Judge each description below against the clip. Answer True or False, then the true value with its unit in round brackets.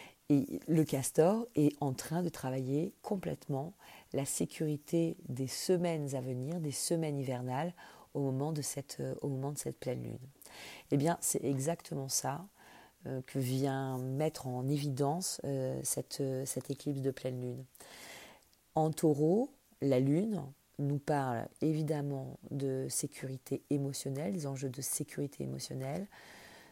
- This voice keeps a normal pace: False (135 wpm)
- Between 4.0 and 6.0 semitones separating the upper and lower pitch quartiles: False (2.9 semitones)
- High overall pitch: False (140 Hz)